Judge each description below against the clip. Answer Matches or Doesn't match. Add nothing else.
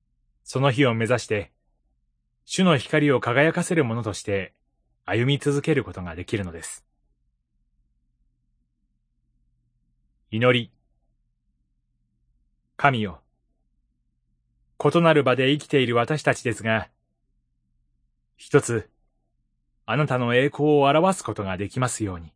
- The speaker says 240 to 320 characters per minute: Doesn't match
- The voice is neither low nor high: Doesn't match